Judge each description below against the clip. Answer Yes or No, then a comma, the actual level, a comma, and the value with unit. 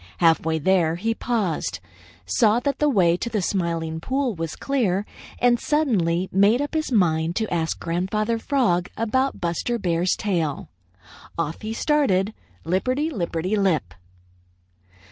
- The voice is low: No, high, 190 Hz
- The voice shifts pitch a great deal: Yes, wide, 5.9 semitones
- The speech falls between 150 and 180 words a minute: No, average, 140 wpm